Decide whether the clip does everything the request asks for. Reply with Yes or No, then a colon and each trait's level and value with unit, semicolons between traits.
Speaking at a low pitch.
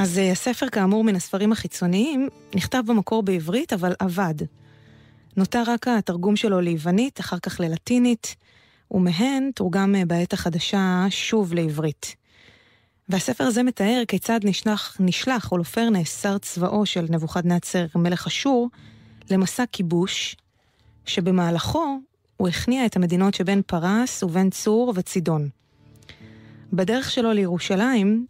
No: high, 190 Hz